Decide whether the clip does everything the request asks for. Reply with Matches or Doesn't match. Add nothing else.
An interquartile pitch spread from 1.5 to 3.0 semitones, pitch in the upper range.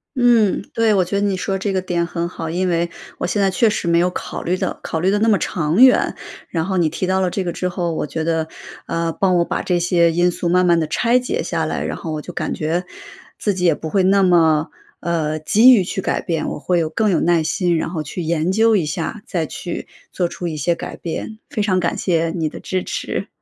Doesn't match